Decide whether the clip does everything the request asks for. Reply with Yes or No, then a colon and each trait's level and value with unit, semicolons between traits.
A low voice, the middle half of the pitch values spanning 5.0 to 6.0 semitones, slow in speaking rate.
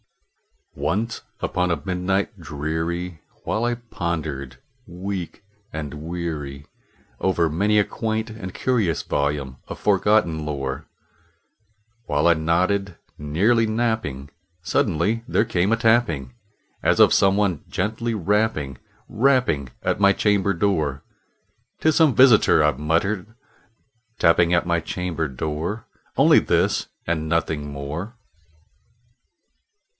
Yes: very low, 90 Hz; wide, 5.5 semitones; slow, 115 wpm